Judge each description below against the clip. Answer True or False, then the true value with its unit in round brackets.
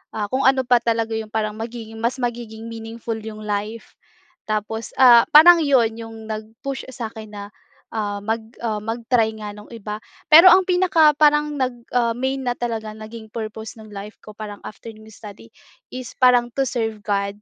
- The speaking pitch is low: False (225 Hz)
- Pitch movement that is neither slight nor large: False (2.3 semitones)